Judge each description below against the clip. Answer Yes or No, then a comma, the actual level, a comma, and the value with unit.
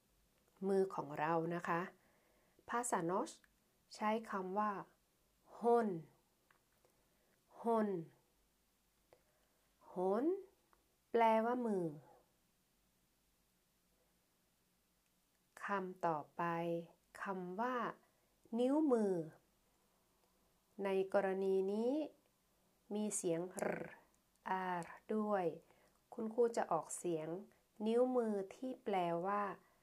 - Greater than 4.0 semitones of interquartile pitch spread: Yes, average, 4.6 semitones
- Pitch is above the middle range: Yes, high, 195 Hz